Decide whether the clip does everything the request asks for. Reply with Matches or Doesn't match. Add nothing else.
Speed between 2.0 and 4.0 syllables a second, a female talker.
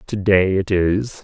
Doesn't match